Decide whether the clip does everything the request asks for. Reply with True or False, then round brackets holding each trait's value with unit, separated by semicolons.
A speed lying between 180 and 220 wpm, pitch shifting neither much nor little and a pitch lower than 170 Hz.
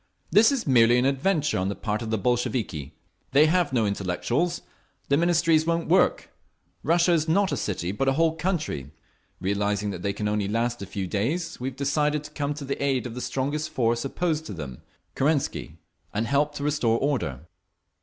False (185 wpm; 6.8 semitones; 135 Hz)